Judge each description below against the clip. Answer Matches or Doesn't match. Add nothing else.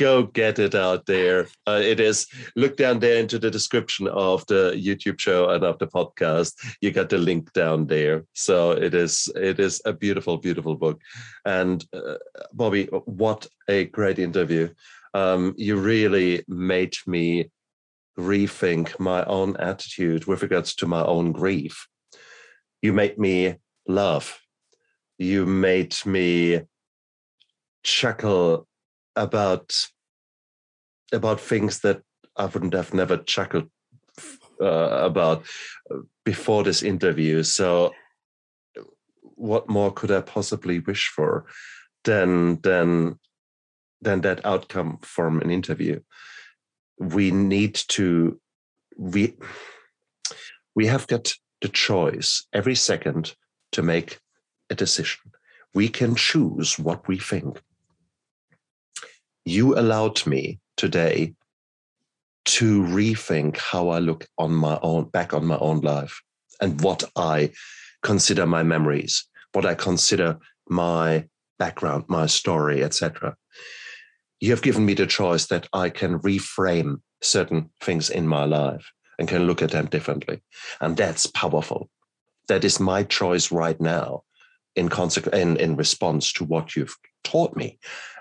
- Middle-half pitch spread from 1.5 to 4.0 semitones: Matches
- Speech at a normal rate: Doesn't match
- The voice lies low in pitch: Matches